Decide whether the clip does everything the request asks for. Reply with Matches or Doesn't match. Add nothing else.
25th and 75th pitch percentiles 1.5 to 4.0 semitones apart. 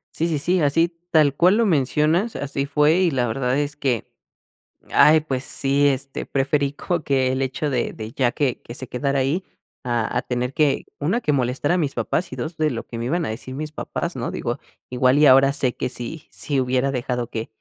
Matches